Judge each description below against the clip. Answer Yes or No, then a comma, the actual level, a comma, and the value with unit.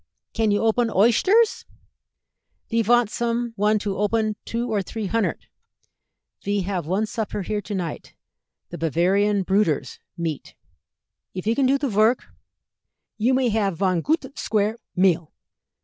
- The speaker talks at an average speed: Yes, average, 145 wpm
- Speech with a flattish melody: No, average, 3.1 semitones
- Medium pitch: No, high, 210 Hz